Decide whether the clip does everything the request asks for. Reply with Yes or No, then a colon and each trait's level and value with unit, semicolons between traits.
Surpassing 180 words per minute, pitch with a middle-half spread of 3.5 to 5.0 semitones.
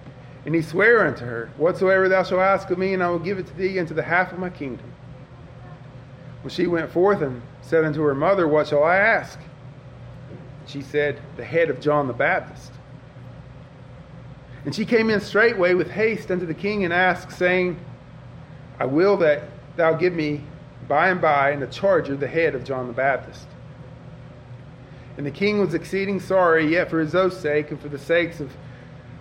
Yes: average, 195 wpm; average, 4.6 semitones